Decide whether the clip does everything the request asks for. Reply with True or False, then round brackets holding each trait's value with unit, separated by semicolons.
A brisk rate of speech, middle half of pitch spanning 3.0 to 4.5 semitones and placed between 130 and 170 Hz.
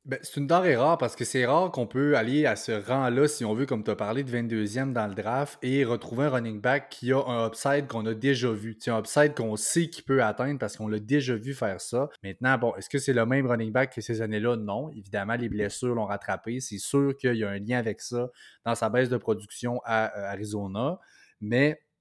False (245 wpm; 3.7 semitones; 120 Hz)